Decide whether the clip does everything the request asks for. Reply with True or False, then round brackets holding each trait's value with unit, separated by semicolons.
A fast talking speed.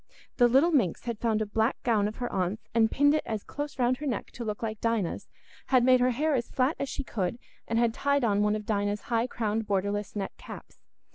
True (230 wpm)